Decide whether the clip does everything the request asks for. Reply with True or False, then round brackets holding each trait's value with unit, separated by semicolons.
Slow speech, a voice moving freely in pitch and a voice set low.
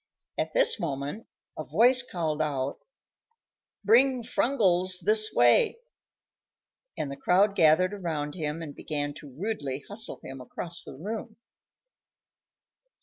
False (120 wpm; 6.6 semitones; 170 Hz)